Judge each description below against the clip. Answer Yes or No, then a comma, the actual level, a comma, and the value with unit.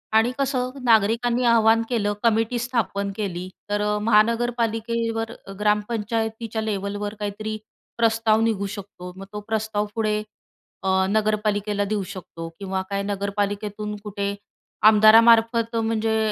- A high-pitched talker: Yes, high, 215 Hz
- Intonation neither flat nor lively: No, narrow, 1.9 semitones